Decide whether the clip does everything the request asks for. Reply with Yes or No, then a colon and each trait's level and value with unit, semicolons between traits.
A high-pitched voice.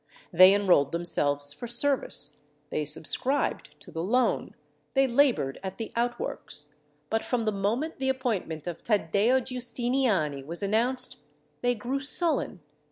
Yes: high, 225 Hz